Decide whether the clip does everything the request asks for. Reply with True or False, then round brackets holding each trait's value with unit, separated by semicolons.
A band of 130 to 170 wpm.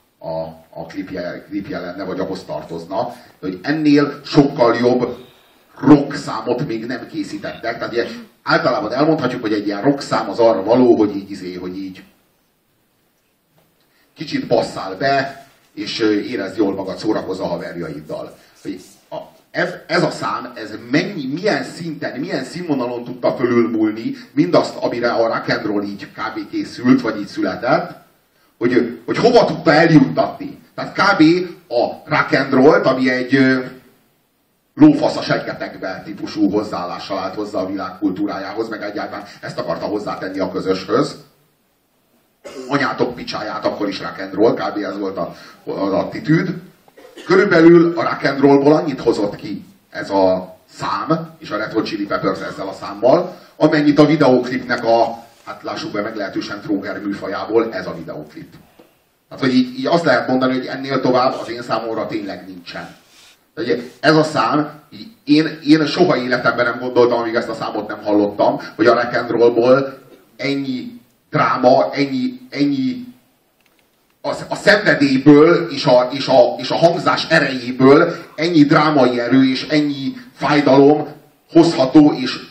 True (140 wpm)